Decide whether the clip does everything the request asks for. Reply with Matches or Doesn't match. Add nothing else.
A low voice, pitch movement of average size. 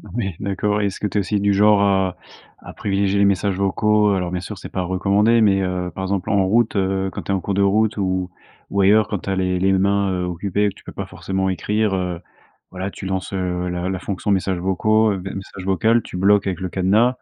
Doesn't match